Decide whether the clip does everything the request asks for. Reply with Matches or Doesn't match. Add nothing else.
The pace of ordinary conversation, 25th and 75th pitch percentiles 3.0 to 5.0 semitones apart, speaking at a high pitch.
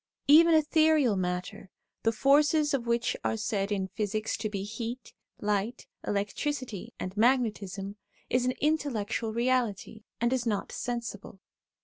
Doesn't match